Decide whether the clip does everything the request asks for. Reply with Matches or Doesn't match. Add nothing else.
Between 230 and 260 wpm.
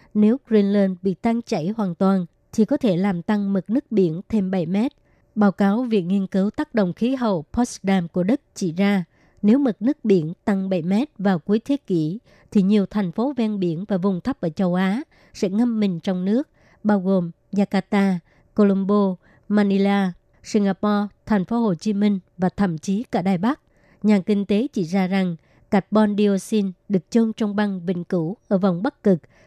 Doesn't match